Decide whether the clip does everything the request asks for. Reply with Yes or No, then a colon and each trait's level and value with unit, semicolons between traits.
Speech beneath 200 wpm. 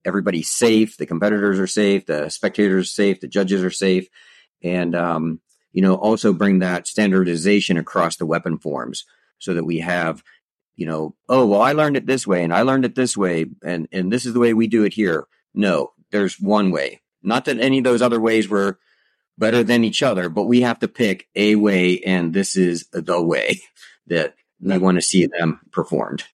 No: fast, 205 wpm